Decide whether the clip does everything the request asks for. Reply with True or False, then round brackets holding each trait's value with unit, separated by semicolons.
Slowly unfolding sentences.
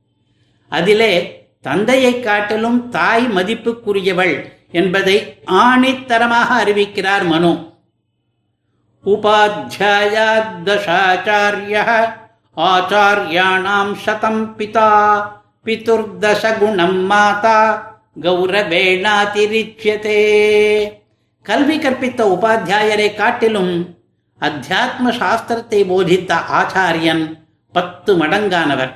True (50 wpm)